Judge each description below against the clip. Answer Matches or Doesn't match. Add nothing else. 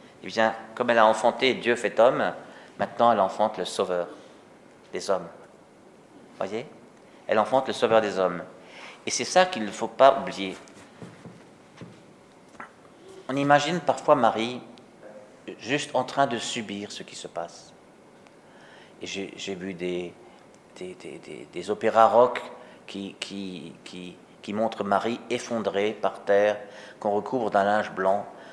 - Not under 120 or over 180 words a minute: Matches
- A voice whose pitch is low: Matches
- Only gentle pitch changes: Doesn't match